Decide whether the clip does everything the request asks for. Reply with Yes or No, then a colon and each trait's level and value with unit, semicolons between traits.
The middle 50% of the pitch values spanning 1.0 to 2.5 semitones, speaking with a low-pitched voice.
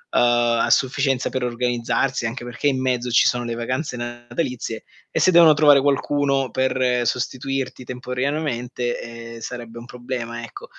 Yes: narrow, 2.1 semitones; low, 125 Hz